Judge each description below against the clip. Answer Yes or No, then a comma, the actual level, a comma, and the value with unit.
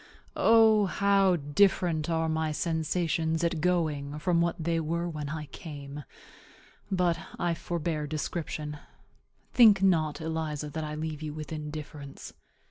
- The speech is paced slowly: Yes, slow, 130 wpm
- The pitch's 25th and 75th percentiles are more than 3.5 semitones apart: No, narrow, 2.4 semitones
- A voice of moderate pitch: Yes, medium, 160 Hz